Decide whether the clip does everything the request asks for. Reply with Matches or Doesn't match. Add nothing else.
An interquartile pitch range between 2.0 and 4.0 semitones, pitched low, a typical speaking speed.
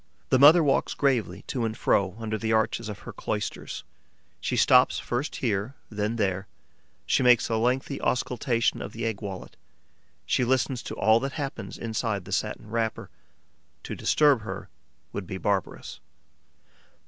Matches